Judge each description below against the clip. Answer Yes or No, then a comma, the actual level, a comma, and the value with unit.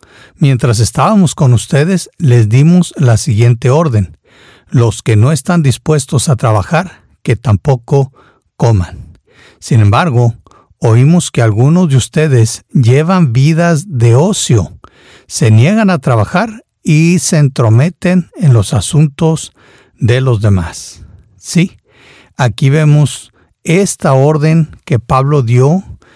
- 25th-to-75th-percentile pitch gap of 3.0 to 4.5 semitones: No, average, 5.3 semitones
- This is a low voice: Yes, low, 130 Hz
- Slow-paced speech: Yes, slow, 115 wpm